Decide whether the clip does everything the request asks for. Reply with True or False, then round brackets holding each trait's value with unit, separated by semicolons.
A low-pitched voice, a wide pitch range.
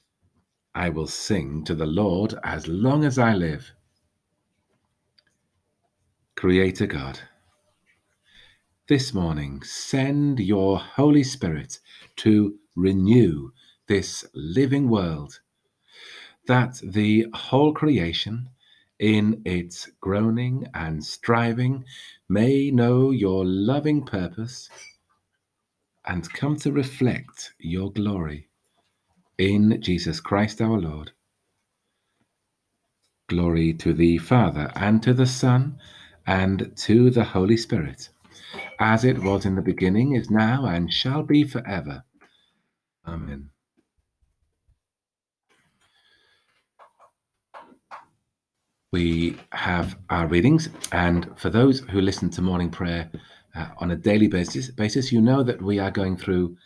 True (100 Hz; 5.9 semitones)